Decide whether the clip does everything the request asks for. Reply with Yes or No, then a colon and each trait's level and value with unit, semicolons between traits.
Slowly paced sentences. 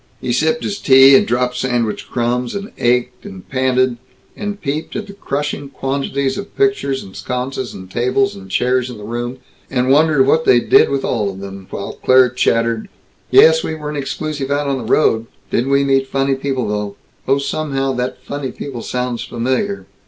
No: average, 185 wpm